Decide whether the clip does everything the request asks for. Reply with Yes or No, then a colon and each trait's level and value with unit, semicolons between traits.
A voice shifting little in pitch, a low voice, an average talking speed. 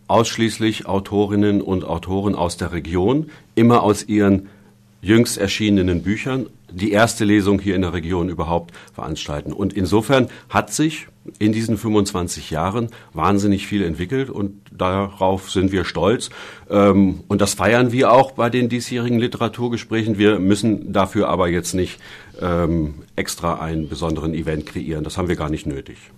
No: average, 3.7 semitones; low, 100 Hz; average, 145 wpm